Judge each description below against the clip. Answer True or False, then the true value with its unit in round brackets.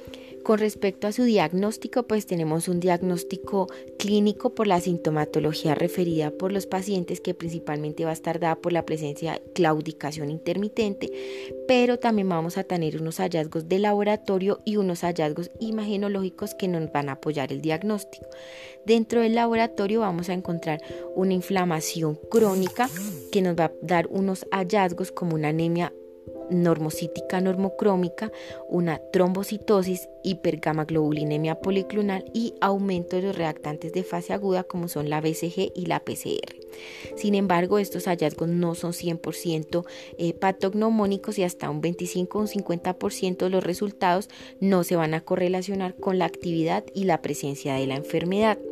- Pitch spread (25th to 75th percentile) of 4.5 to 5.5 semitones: False (3.5 semitones)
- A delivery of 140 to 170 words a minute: True (150 wpm)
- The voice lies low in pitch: False (180 Hz)